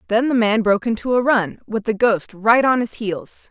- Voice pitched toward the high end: Yes, high, 220 Hz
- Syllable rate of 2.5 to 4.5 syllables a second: No, 4.9 syllables/s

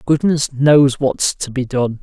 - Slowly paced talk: No, average, 180 wpm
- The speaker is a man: Yes, male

